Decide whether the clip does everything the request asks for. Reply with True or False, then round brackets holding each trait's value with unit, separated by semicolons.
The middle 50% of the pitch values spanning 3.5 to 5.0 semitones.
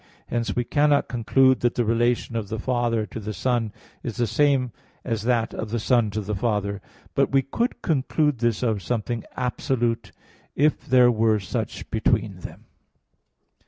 False (2.5 semitones)